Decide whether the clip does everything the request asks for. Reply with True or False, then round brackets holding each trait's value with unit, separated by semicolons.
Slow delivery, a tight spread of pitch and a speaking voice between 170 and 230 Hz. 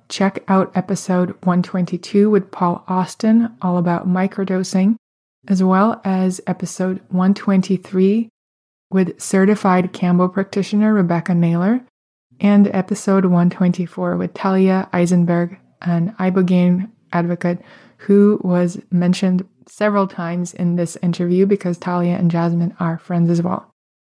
True (115 wpm; 1.7 semitones; 185 Hz)